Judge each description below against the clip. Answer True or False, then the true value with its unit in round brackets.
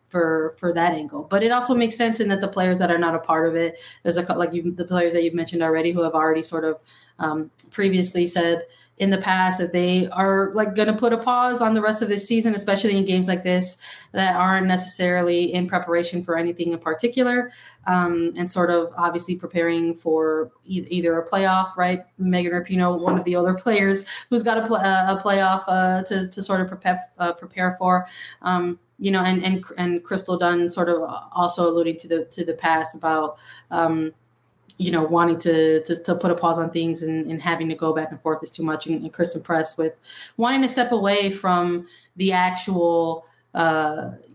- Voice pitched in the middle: True (175 Hz)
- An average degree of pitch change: False (2.2 semitones)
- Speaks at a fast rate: True (215 wpm)